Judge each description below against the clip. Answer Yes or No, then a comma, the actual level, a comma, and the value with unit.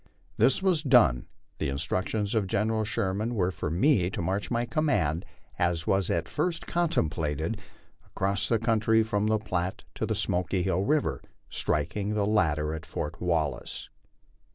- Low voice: Yes, low, 100 Hz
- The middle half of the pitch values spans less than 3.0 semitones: No, average, 4.7 semitones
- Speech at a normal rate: Yes, average, 155 wpm